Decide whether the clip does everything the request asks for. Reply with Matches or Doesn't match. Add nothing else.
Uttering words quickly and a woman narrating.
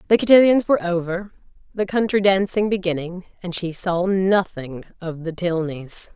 Doesn't match